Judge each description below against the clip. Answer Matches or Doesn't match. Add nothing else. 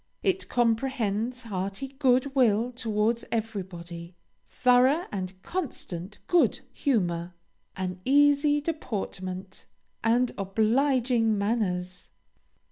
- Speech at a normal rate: Doesn't match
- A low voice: Doesn't match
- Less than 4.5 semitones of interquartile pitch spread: Doesn't match